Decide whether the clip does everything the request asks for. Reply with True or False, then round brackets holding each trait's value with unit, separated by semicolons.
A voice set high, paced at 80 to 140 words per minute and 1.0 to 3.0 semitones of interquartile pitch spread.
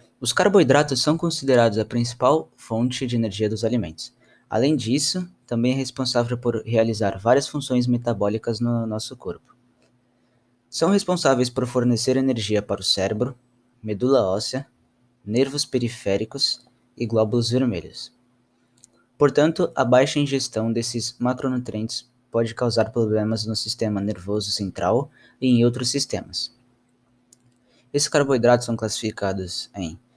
False (120 Hz; 120 wpm; 2.5 semitones)